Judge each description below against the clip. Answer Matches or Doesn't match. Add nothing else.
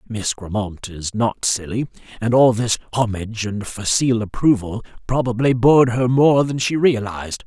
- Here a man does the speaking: Matches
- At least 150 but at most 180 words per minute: Matches